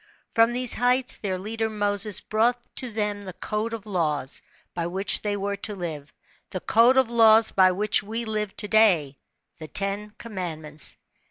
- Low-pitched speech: No, high, 210 Hz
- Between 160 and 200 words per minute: Yes, average, 170 wpm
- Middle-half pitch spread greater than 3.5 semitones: No, average, 3.2 semitones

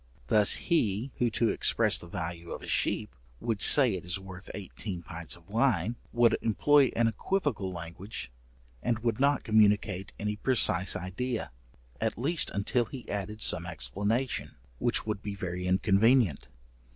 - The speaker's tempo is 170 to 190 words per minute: No, average, 150 wpm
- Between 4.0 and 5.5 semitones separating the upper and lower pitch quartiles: Yes, average, 4.5 semitones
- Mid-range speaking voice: No, low, 105 Hz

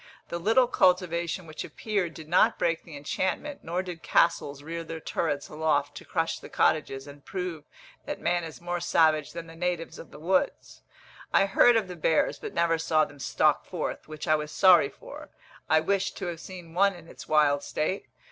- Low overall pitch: No, medium, 165 Hz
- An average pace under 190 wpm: No, average, 195 wpm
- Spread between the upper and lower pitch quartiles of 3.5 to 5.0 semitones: No, narrow, 2.5 semitones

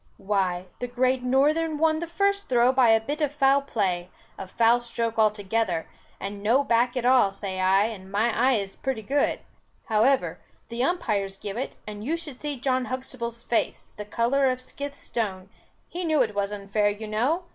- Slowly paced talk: No, average, 190 wpm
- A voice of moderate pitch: No, high, 235 Hz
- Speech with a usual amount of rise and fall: Yes, average, 4.6 semitones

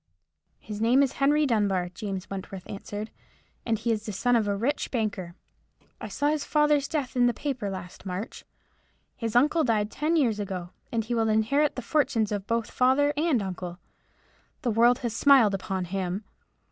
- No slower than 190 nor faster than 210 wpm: No, average, 180 wpm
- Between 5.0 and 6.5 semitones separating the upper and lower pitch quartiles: Yes, average, 5.3 semitones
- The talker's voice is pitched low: No, high, 225 Hz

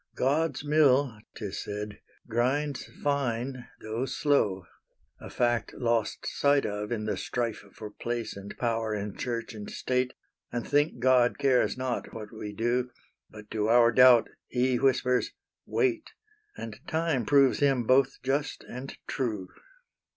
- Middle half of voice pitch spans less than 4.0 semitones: Yes, average, 3.3 semitones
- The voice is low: Yes, low, 125 Hz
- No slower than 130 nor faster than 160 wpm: Yes, average, 140 wpm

